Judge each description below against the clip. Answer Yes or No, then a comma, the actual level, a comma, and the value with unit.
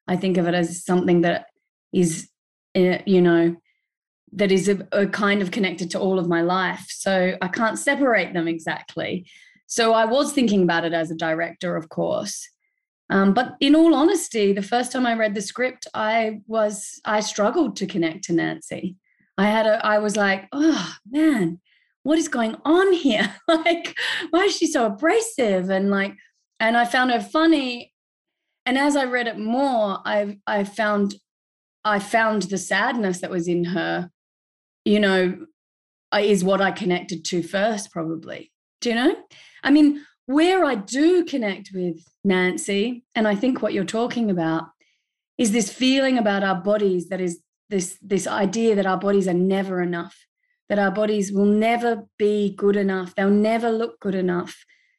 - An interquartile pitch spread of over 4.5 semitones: Yes, average, 4.9 semitones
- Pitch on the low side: No, high, 205 Hz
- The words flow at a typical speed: No, fast, 175 wpm